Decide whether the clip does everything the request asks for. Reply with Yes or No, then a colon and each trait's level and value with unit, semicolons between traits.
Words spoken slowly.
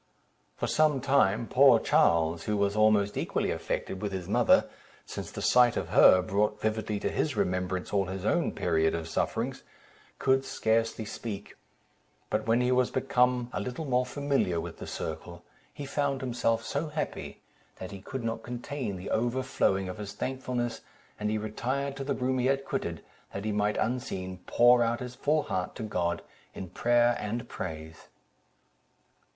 No: average, 170 wpm